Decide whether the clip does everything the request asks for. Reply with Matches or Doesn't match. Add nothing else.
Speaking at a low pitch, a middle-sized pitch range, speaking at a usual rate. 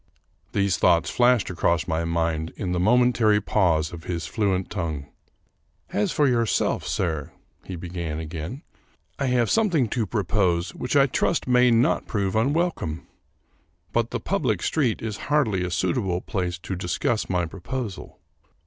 Doesn't match